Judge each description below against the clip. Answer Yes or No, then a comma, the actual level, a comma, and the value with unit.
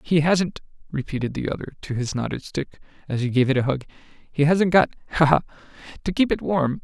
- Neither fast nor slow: Yes, average, 185 wpm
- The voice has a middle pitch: Yes, medium, 150 Hz